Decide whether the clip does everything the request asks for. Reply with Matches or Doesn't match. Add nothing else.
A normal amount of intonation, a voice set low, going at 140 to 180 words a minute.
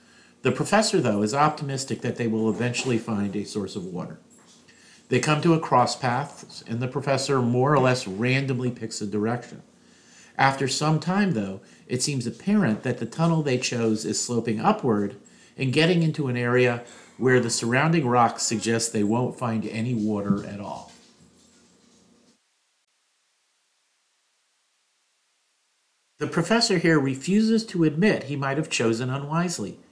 Matches